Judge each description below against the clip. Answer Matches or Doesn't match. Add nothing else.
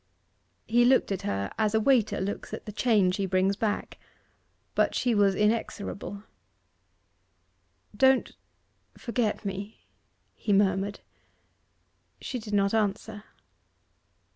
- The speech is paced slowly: Matches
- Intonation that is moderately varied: Doesn't match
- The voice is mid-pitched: Doesn't match